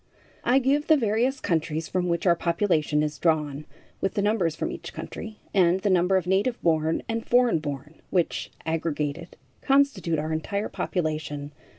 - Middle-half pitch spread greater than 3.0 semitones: Yes, average, 5.0 semitones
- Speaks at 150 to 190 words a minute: Yes, average, 165 wpm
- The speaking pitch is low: No, medium, 170 Hz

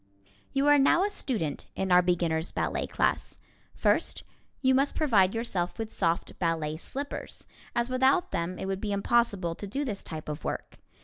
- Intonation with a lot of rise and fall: Yes, wide, 7.2 semitones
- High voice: Yes, high, 200 Hz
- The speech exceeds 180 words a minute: No, average, 175 wpm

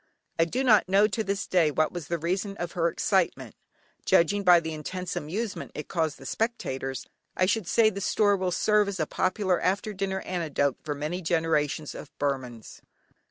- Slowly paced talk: No, average, 185 wpm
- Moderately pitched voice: Yes, medium, 180 Hz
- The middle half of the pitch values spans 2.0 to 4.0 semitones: No, average, 4.4 semitones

